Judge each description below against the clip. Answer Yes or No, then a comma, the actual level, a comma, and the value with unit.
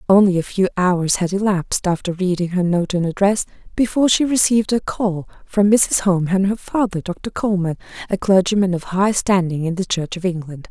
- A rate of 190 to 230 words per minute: Yes, average, 195 wpm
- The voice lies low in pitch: No, high, 190 Hz